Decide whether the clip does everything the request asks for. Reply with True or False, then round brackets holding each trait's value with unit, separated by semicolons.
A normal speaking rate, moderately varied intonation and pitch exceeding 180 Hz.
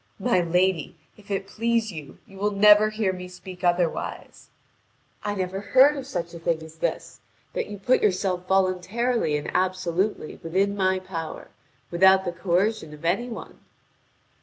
True (160 wpm; 3.0 semitones; 190 Hz)